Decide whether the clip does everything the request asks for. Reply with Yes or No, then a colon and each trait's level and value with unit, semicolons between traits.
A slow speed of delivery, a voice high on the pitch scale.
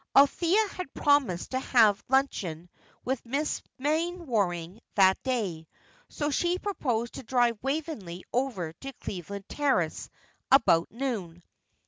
Yes: slow, 115 wpm; high, 245 Hz